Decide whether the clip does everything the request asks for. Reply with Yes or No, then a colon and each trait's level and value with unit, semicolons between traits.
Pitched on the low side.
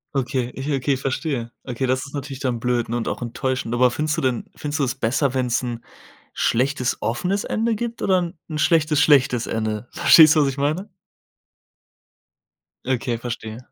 Yes: low, 130 Hz